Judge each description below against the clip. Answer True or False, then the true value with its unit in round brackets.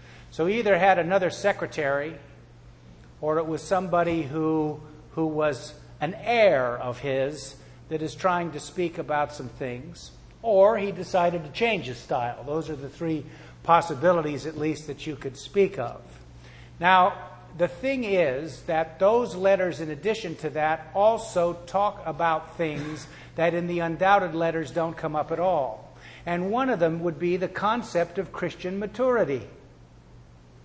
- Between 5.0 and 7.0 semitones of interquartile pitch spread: False (4.4 semitones)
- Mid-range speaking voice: True (160 Hz)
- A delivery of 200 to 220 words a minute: False (155 wpm)